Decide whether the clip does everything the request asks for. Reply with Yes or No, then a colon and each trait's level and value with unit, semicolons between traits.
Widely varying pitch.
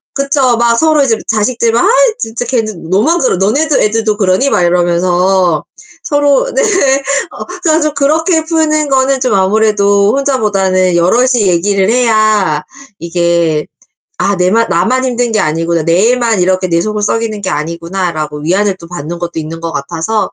Yes: wide, 6.5 semitones